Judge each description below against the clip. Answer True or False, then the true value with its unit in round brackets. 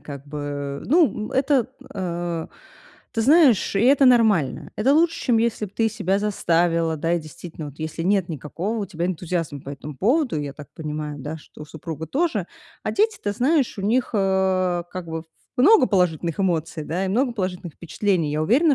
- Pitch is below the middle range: False (185 Hz)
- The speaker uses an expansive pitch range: True (6.2 semitones)